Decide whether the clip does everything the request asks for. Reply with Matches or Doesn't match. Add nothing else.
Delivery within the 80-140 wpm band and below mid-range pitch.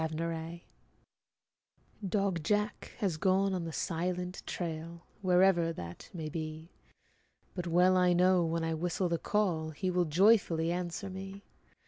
Doesn't match